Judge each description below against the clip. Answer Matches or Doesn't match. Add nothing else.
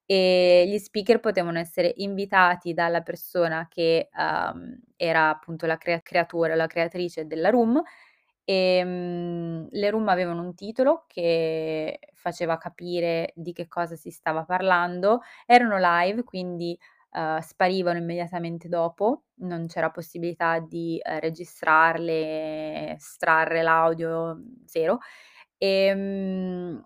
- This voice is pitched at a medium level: Matches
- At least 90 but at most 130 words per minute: Matches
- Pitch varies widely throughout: Doesn't match